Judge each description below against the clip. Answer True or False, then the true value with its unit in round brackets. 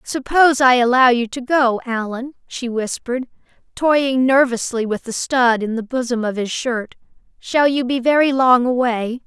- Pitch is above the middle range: True (250 Hz)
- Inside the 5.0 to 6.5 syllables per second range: False (4.6 syllables/s)